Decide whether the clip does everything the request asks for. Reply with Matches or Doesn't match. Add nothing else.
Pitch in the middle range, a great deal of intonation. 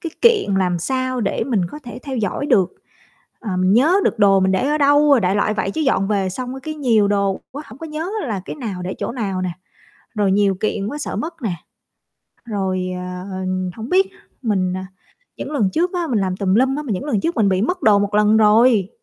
Doesn't match